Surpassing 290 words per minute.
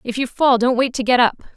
Yes: fast, 310 wpm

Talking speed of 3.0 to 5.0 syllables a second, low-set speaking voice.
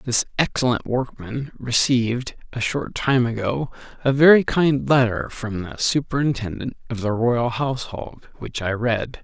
Yes: 4.3 syllables/s; low, 125 Hz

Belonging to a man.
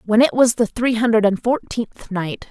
No: female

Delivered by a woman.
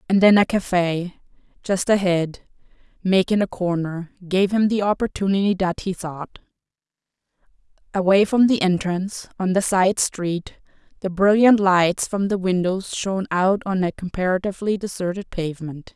Yes: female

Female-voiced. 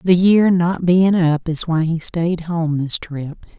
Yes: female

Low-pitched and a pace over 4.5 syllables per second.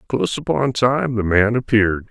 Yes: low, 115 Hz; 5.2 syllables/s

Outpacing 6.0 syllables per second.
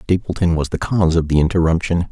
Yes: 6.6 syllables/s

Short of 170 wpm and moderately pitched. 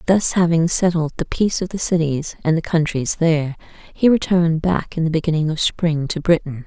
No: average, 200 wpm; medium, 165 Hz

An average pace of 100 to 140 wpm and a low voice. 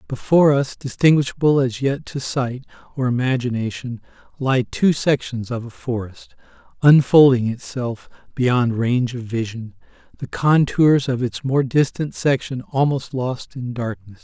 Yes: slow, 135 wpm; low, 130 Hz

